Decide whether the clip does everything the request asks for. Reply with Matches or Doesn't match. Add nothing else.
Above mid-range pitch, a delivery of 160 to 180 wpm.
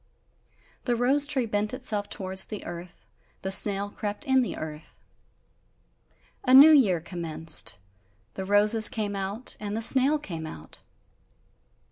Doesn't match